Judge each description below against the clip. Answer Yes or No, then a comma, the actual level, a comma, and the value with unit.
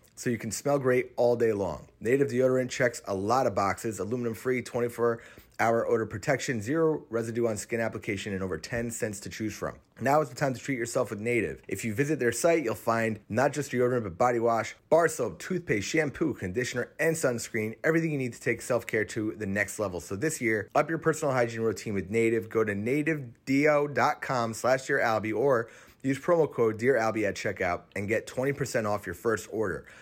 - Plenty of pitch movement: No, average, 3.7 semitones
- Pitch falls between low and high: No, low, 120 Hz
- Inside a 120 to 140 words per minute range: No, fast, 205 wpm